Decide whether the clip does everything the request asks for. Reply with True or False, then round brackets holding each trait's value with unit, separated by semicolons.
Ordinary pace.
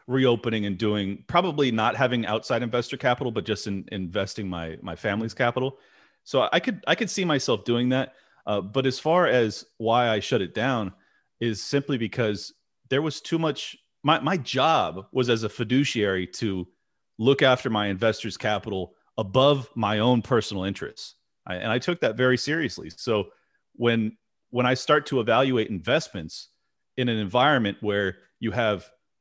True (170 wpm)